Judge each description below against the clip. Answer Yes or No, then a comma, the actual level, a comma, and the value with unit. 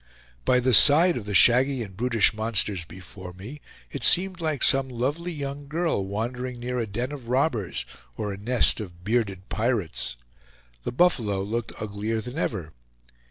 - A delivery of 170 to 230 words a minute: No, average, 160 wpm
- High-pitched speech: No, low, 120 Hz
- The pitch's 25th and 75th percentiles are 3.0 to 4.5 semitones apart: No, average, 5.0 semitones